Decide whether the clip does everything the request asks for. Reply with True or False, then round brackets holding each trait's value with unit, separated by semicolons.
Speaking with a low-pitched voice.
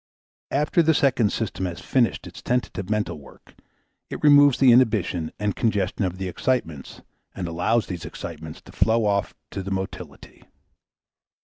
True (105 Hz)